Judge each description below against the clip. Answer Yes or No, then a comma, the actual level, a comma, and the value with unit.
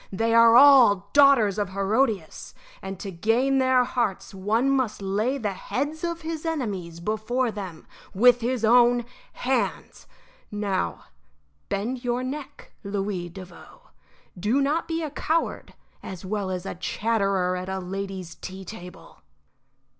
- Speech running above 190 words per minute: No, average, 140 wpm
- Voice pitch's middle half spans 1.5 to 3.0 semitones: No, average, 5.1 semitones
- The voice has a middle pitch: No, high, 215 Hz